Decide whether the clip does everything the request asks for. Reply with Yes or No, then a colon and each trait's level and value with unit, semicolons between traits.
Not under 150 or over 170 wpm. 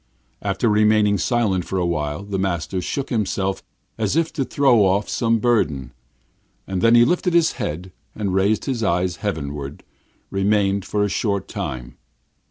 Yes: average, 160 wpm